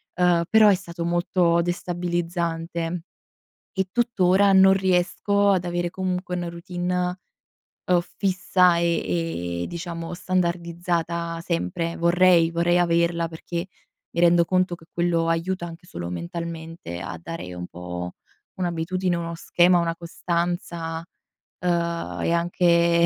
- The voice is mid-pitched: Yes, medium, 170 Hz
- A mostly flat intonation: Yes, narrow, 1.3 semitones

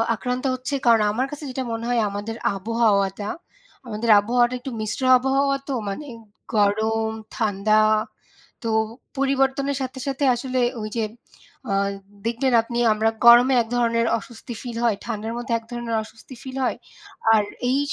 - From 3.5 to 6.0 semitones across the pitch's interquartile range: No, average, 2.8 semitones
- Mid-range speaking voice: No, high, 235 Hz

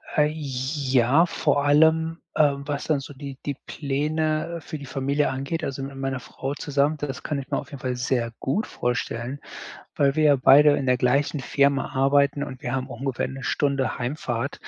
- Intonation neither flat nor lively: No, narrow, 2.0 semitones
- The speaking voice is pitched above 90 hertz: Yes, medium, 140 Hz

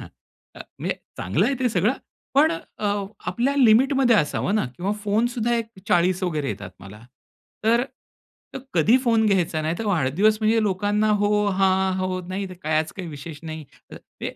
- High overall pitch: Yes, high, 200 Hz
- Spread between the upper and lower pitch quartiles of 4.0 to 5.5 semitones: Yes, average, 4.5 semitones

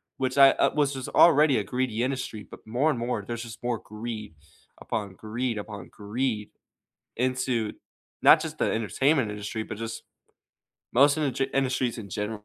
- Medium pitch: No, low, 120 Hz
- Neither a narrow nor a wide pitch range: Yes, average, 3.5 semitones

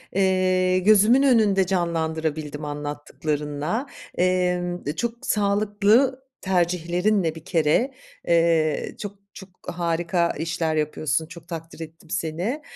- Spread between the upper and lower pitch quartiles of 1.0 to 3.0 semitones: No, average, 3.8 semitones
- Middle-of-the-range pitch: Yes, medium, 175 Hz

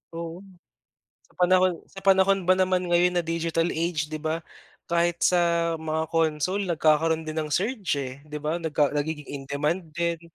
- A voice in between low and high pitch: Yes, medium, 165 Hz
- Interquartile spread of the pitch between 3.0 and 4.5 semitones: No, narrow, 2.4 semitones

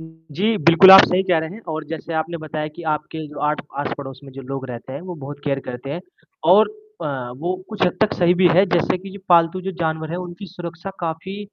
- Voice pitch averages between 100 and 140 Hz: No, medium, 165 Hz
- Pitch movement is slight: No, average, 3.1 semitones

